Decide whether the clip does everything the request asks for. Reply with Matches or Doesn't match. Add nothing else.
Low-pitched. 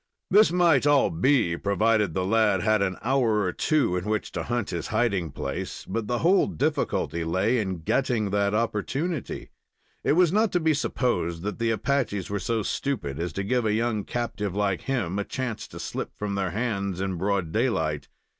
Matches